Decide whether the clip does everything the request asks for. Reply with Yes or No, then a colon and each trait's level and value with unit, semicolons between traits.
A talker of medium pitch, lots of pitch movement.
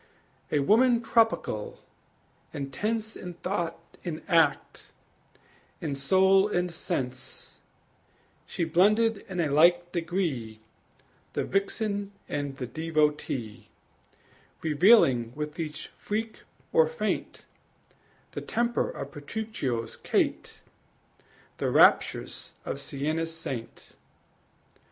Yes: medium, 165 Hz; wide, 6.1 semitones